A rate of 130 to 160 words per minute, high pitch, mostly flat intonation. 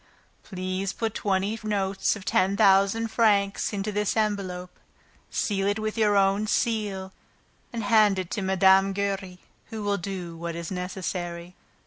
Yes: average, 150 wpm; high, 195 Hz; narrow, 1.8 semitones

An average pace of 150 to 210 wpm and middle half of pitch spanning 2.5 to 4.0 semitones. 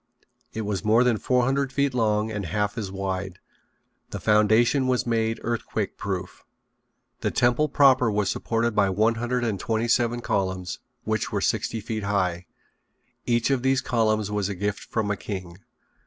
Yes: average, 170 wpm; average, 3.1 semitones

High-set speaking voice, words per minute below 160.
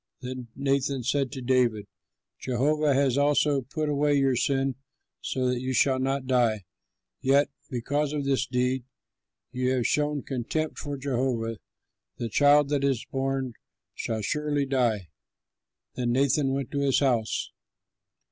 No: low, 135 Hz; average, 140 wpm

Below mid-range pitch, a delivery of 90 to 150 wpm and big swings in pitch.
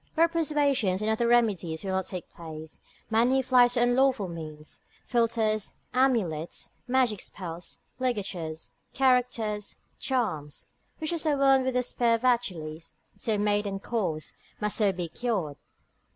No: high, 220 Hz; average, 145 wpm; wide, 5.8 semitones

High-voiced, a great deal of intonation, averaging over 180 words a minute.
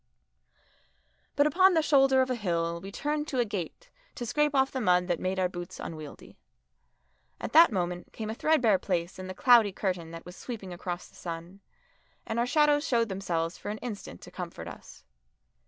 Yes: high, 205 Hz; wide, 6.9 semitones; average, 190 wpm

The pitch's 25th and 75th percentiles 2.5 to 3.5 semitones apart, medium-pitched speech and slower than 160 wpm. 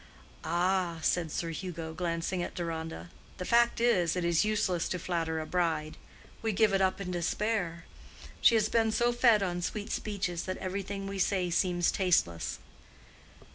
No: average, 3.2 semitones; medium, 180 Hz; average, 170 wpm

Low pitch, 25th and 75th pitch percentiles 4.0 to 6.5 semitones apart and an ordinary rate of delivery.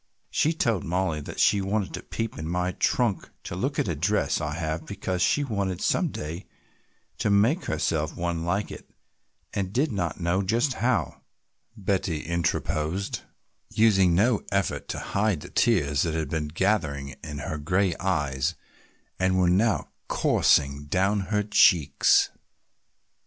Yes: very low, 90 Hz; average, 4.4 semitones; average, 150 wpm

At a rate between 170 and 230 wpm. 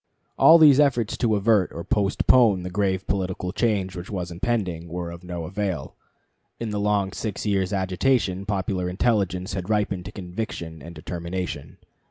No: average, 160 wpm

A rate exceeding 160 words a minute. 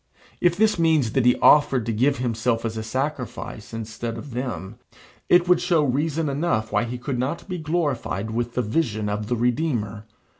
Yes: average, 185 wpm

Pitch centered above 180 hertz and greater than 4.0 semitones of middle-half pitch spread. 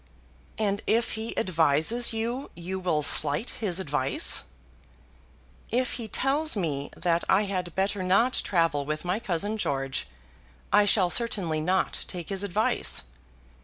Yes: high, 190 Hz; average, 5.0 semitones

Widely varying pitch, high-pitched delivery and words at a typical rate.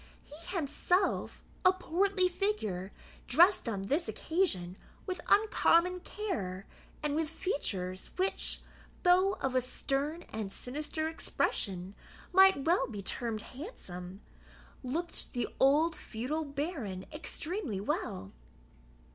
No: wide, 8.9 semitones; very high, 295 Hz; slow, 110 wpm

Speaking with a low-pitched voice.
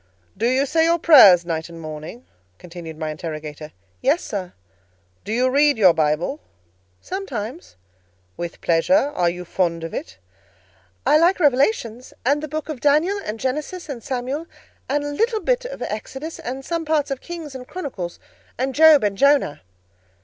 No: very high, 260 Hz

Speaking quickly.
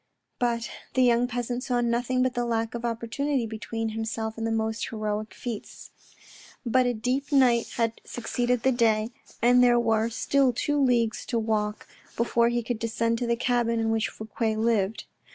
No: average, 175 wpm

